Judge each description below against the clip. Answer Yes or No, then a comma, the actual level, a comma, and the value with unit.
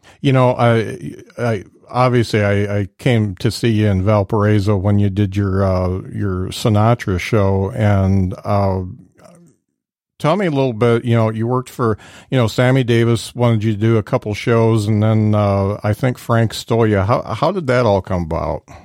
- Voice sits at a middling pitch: No, low, 110 Hz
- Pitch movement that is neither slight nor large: Yes, average, 3.2 semitones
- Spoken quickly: No, average, 190 wpm